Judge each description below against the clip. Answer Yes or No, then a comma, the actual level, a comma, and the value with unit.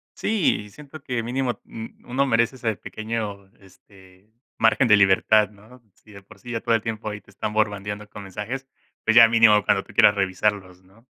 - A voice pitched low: Yes, low, 110 Hz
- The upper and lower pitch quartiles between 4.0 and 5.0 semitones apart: No, narrow, 2.5 semitones